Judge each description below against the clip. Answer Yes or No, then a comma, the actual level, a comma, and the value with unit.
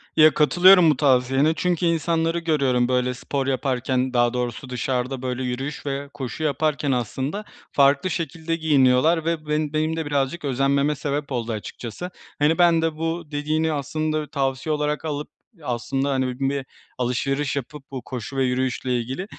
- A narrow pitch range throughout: No, average, 3.4 semitones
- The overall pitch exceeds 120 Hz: Yes, medium, 140 Hz